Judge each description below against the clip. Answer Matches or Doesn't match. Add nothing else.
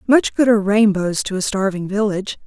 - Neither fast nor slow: Matches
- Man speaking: Doesn't match